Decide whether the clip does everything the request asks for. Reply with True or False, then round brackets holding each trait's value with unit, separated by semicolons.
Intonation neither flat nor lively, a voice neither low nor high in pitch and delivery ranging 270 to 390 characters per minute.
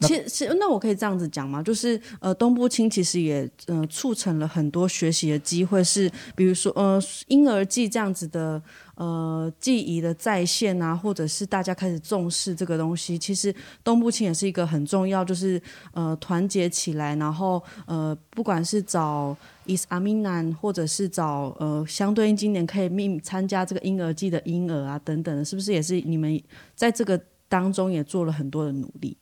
True (3.5 semitones; 180 Hz; 300 characters per minute)